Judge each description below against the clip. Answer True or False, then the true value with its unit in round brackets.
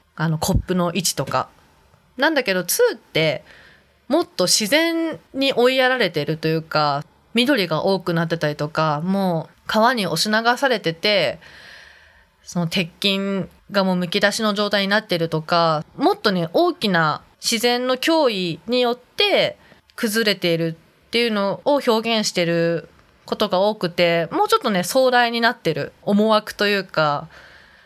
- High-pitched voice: True (200 Hz)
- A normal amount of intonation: False (6.2 semitones)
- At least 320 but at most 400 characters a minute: False (295 characters per minute)